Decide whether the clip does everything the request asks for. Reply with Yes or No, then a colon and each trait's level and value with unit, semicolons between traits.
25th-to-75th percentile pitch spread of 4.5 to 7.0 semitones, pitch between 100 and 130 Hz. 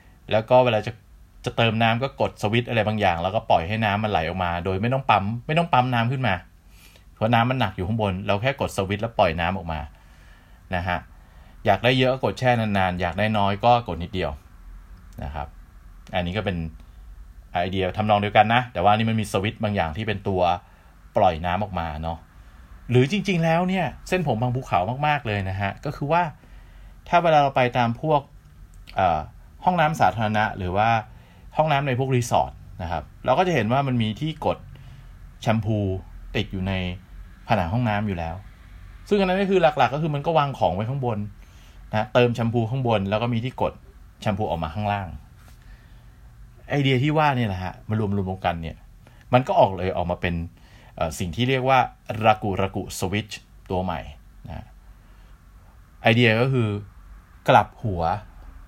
Yes: average, 5.2 semitones; low, 105 Hz